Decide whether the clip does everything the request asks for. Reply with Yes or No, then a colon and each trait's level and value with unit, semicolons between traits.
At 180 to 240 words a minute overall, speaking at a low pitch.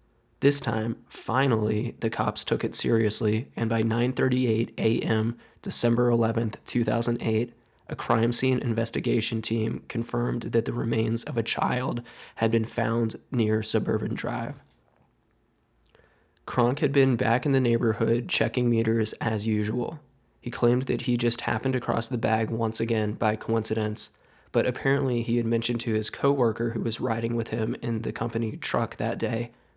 No: average, 155 wpm; low, 115 Hz